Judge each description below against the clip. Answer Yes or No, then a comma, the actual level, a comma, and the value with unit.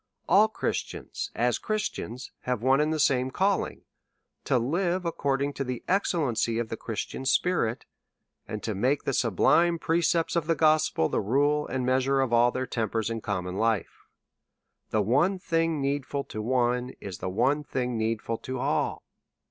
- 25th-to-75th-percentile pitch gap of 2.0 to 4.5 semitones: No, average, 5.2 semitones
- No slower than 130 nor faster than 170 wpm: Yes, average, 165 wpm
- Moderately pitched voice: No, low, 130 Hz